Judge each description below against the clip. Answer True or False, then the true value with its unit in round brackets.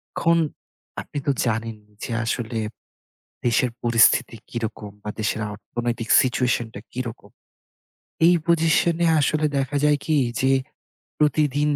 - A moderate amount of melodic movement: True (4.6 semitones)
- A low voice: True (125 Hz)